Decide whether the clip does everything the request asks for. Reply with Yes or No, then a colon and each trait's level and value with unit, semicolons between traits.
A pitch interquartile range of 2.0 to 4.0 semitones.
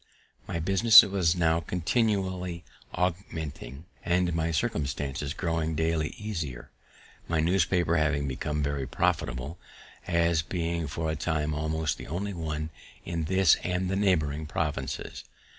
Yes: average, 3.0 semitones